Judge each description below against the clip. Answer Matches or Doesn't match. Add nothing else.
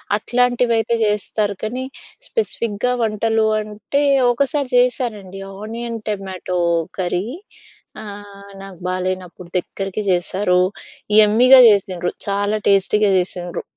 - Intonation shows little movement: Doesn't match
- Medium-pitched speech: Doesn't match